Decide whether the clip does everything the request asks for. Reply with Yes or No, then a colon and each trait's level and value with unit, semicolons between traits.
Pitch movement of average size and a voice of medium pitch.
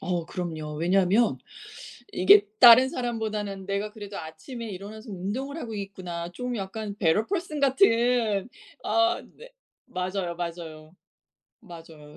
No: average, 5.0 semitones; high, 200 Hz